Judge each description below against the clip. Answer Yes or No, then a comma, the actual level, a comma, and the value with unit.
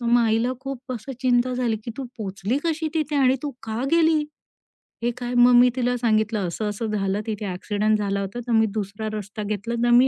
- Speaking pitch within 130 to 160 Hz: No, high, 235 Hz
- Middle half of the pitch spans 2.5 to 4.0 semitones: Yes, average, 3.2 semitones